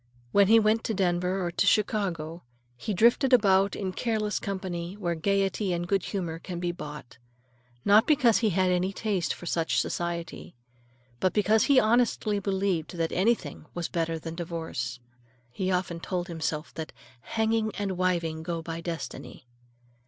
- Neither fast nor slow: Yes, average, 160 wpm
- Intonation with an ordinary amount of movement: Yes, average, 3.6 semitones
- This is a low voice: No, medium, 185 Hz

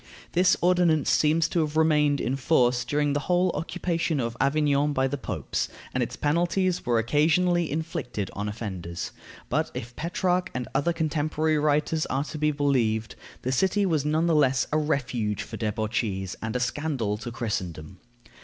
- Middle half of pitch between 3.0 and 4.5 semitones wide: No, average, 4.9 semitones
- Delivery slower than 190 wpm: Yes, average, 165 wpm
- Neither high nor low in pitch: Yes, medium, 145 Hz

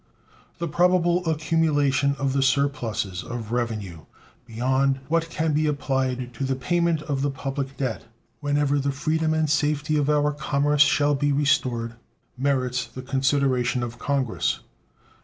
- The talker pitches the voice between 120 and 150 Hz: Yes, medium, 140 Hz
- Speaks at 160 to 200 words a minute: No, average, 140 wpm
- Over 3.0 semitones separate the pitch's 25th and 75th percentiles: No, narrow, 2.6 semitones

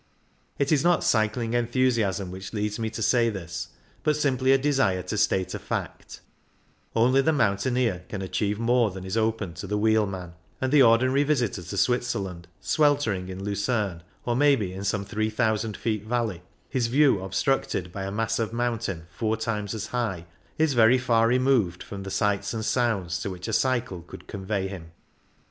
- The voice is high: No, low, 110 Hz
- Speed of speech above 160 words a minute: Yes, average, 180 wpm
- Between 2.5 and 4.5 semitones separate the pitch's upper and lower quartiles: Yes, average, 4.2 semitones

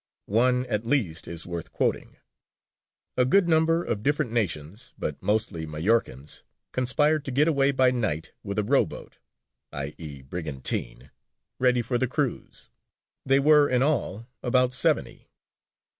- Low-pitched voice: Yes, low, 120 Hz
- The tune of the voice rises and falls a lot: Yes, wide, 7.9 semitones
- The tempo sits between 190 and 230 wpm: No, average, 140 wpm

